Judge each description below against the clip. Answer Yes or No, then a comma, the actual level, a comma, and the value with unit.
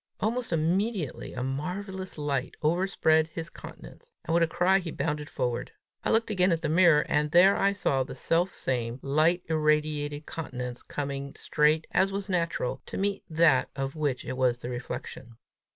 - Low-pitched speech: No, medium, 155 Hz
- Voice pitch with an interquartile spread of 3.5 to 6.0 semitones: Yes, average, 4.7 semitones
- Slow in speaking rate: No, average, 170 wpm